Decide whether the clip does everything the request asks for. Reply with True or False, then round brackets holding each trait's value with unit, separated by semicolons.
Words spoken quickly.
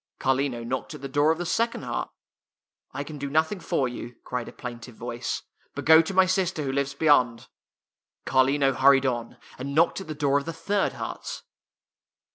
True (210 wpm)